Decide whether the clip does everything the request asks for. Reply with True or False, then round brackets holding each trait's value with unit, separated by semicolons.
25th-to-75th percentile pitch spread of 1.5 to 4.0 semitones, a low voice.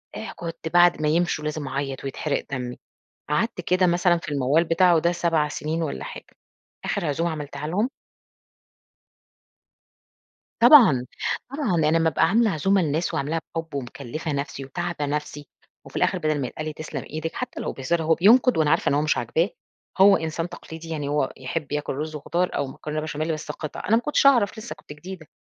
False (3.0 semitones; 160 Hz)